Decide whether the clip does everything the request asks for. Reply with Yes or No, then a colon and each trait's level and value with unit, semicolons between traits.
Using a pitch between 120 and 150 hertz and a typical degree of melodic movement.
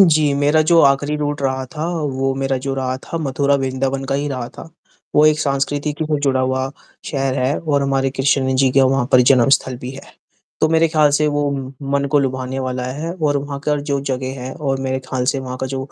No: low, 135 Hz; narrow, 1.9 semitones